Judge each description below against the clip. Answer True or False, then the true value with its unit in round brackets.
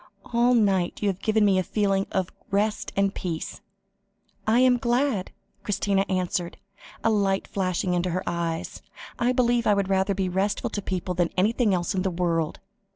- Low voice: False (195 Hz)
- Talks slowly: False (175 wpm)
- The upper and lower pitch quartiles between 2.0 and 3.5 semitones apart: True (2.8 semitones)